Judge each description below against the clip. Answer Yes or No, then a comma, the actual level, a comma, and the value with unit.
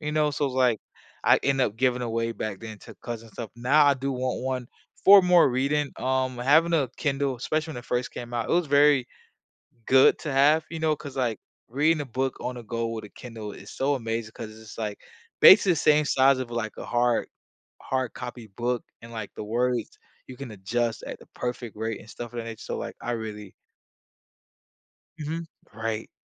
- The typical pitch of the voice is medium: No, low, 125 Hz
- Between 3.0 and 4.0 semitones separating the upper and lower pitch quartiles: Yes, average, 3.4 semitones